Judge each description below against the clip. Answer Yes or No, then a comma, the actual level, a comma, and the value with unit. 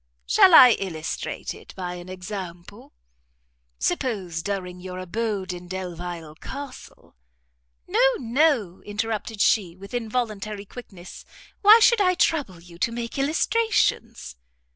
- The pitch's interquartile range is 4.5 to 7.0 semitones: Yes, average, 5.2 semitones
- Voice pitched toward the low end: No, high, 200 Hz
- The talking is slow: Yes, slow, 120 wpm